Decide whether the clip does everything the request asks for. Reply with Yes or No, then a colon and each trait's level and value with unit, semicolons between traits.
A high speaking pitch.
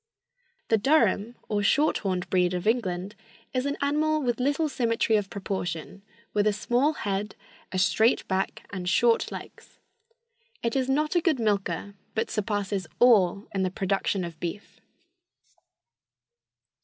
Yes: high, 210 Hz